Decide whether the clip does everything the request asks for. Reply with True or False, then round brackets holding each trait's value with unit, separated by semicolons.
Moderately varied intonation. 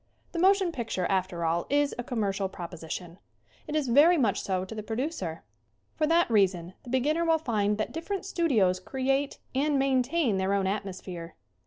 False (7.9 semitones)